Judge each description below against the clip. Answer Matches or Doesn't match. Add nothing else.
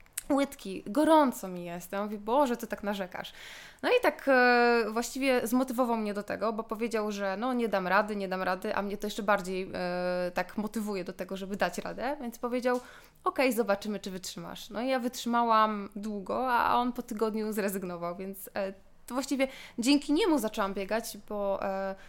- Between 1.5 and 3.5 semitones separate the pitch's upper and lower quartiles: Doesn't match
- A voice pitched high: Matches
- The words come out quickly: Matches